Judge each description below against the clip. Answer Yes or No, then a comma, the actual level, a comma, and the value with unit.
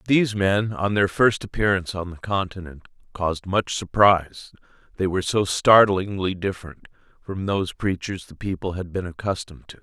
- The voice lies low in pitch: Yes, very low, 95 Hz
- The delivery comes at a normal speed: Yes, average, 160 wpm